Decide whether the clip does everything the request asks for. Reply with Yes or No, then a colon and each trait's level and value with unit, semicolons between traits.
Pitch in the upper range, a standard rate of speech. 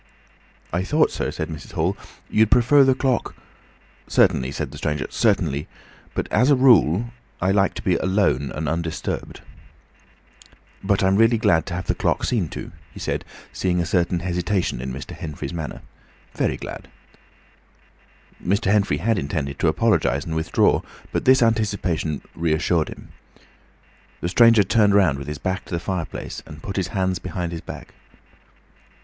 No: very low, 90 Hz; average, 160 wpm